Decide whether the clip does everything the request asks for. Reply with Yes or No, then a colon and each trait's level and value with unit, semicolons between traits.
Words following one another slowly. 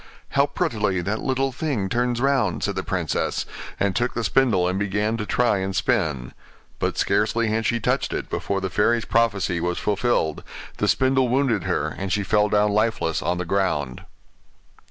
No: average, 175 wpm